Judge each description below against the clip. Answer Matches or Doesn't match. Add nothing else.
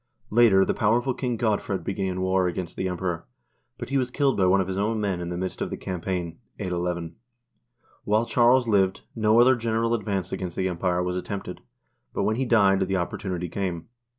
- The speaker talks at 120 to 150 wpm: Doesn't match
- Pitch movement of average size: Matches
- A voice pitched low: Matches